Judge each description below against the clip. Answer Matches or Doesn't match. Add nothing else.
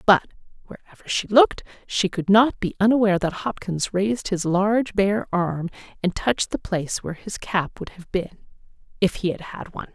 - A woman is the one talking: Matches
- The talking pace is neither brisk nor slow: Matches